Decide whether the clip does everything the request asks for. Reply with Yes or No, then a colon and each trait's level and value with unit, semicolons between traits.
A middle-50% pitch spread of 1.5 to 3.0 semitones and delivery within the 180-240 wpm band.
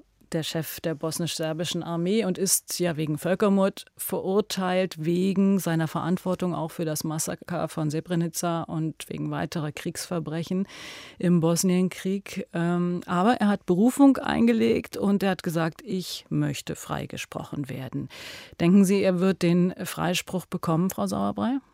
No: narrow, 2.6 semitones; average, 130 wpm